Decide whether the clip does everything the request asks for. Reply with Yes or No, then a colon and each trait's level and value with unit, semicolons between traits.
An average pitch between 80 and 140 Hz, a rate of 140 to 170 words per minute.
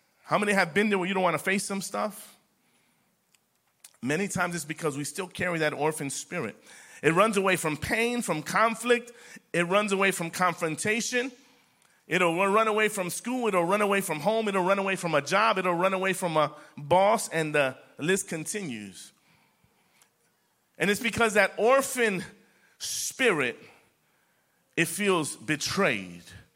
No: high, 190 Hz; average, 160 wpm